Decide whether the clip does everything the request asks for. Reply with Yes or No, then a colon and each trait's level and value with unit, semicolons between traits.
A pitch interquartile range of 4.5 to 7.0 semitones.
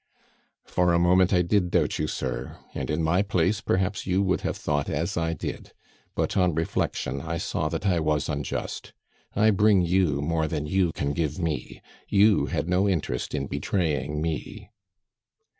No: average, 3.7 semitones